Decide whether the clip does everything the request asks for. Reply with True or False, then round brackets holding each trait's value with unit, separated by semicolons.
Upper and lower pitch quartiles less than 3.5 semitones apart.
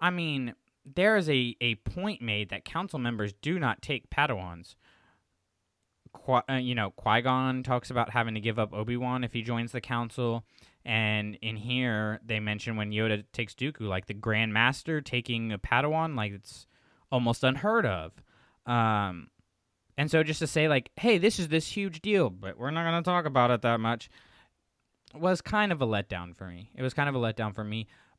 False (4.1 semitones)